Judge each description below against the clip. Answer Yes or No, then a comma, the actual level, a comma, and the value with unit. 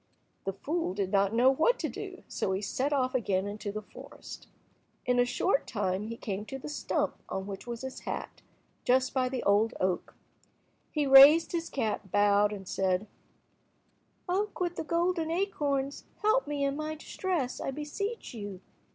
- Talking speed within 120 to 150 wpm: No, average, 175 wpm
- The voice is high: Yes, very high, 255 Hz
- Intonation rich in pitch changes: Yes, wide, 6.9 semitones